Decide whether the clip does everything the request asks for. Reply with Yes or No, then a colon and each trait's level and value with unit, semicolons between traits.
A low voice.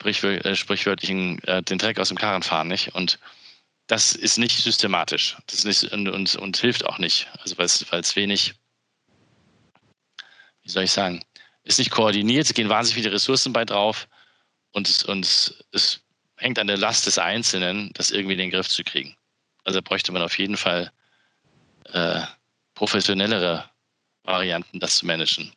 Yes: low, 100 Hz